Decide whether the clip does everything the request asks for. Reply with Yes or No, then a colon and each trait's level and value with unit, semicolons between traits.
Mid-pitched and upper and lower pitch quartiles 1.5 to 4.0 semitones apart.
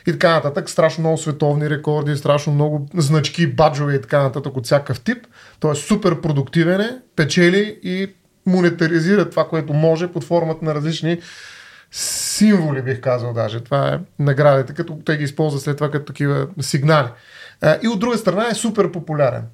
Yes: medium, 155 Hz; average, 3.4 semitones